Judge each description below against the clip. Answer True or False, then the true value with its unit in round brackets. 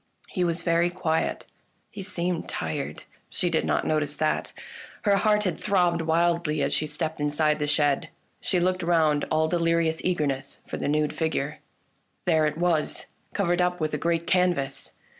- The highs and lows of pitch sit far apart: False (2.6 semitones)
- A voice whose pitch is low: False (165 Hz)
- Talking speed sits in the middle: True (170 wpm)